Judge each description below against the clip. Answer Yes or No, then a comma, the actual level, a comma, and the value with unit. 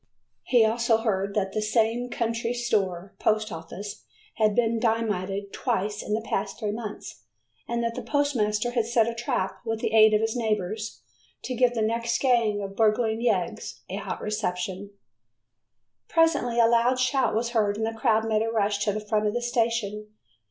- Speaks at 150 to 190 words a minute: Yes, average, 180 wpm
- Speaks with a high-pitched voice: Yes, high, 220 Hz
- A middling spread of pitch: No, narrow, 2.0 semitones